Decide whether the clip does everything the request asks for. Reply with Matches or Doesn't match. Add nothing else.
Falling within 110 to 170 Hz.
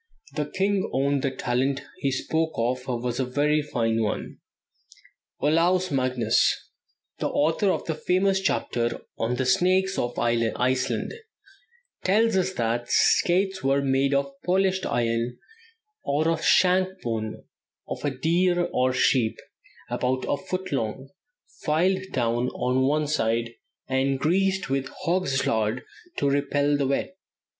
Matches